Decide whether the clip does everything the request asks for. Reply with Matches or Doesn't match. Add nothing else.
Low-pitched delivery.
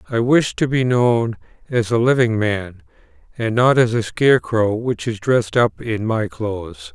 Matches